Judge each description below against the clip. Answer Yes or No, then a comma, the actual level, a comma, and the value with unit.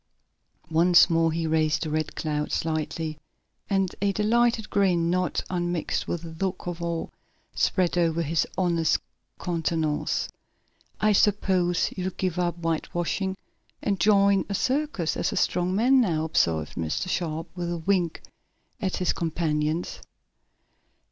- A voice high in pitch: No, medium, 175 Hz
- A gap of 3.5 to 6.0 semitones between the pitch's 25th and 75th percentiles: No, average, 2.8 semitones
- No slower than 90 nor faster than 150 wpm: Yes, slow, 135 wpm